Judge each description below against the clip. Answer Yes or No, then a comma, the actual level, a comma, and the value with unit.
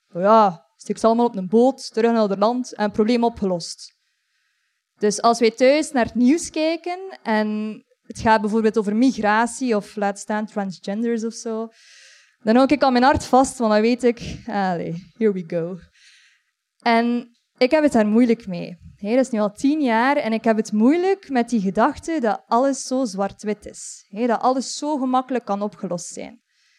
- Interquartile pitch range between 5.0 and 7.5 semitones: No, average, 3.4 semitones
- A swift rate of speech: No, average, 185 wpm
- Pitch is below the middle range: No, high, 230 Hz